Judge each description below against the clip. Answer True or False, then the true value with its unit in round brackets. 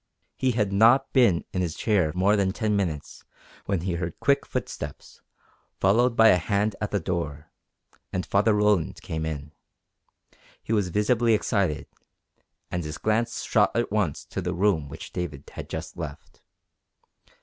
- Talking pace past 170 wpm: False (160 wpm)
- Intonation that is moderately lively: True (4.1 semitones)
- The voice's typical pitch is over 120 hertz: False (100 Hz)